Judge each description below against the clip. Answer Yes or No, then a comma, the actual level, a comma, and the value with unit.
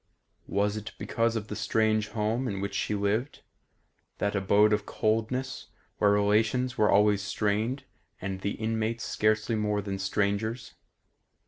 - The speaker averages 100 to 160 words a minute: Yes, average, 140 wpm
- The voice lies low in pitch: Yes, low, 105 Hz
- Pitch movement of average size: No, narrow, 1.6 semitones